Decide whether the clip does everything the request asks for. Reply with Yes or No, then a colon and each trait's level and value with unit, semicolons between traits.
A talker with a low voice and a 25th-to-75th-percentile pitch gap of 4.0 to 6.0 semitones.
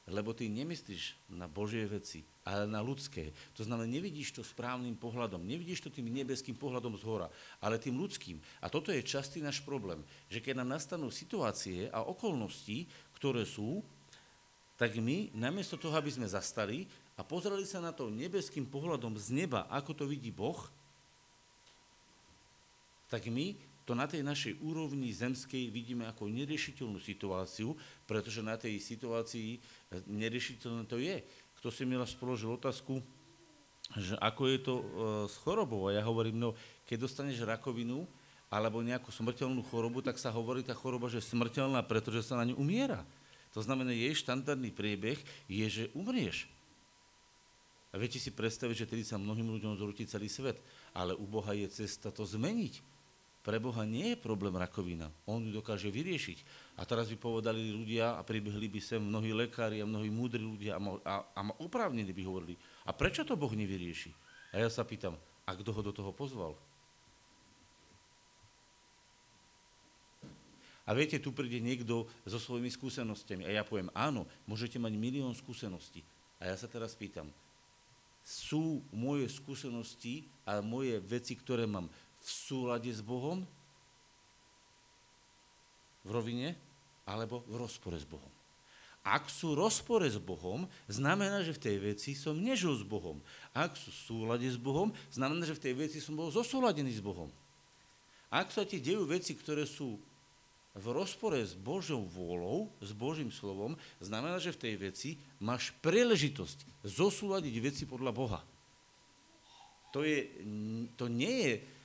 Yes: low, 120 Hz; average, 4.4 semitones